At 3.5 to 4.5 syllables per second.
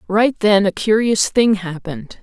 Yes: 4.4 syllables/s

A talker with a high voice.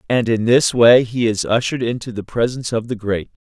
No: low, 115 Hz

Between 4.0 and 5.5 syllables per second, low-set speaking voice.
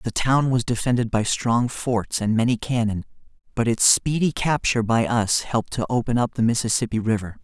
Yes: 5.3 syllables/s; low, 120 Hz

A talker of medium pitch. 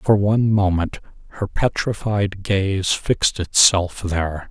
No: very low, 95 Hz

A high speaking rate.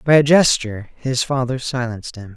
No: average, 180 wpm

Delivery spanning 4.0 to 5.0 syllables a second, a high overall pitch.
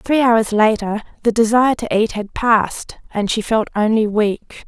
Yes: 4.5 syllables/s; high, 220 Hz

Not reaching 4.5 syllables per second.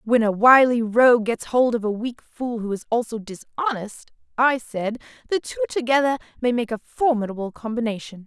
No: 5.0 syllables/s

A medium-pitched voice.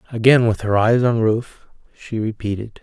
No: low, 115 Hz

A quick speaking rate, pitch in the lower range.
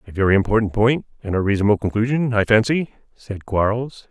No: average, 175 wpm; low, 110 Hz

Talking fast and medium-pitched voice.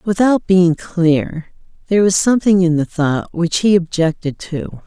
No: average, 160 wpm; medium, 175 Hz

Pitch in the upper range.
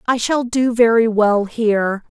Yes: high, 225 Hz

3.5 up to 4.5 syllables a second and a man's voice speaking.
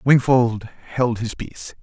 Yes: 4.0 syllables/s; male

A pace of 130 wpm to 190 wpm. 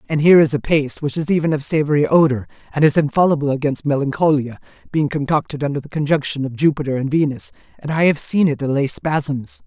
No: average, 200 wpm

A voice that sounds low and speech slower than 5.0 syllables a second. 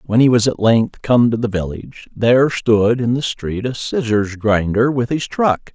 Yes: low, 115 Hz; 4.5 syllables/s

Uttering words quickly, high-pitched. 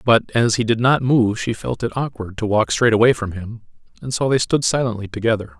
No: fast, 235 wpm; low, 115 Hz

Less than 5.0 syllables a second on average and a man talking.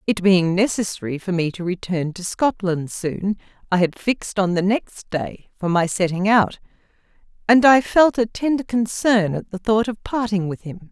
No: 4.6 syllables/s; female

